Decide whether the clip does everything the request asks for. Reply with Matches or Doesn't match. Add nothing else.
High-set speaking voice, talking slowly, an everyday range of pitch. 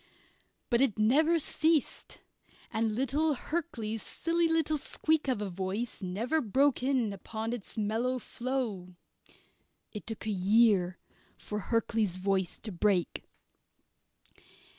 Matches